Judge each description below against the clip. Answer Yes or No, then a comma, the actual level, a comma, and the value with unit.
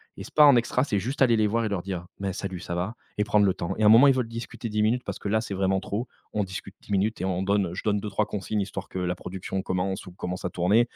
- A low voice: Yes, low, 100 Hz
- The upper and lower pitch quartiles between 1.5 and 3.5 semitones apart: Yes, average, 2.7 semitones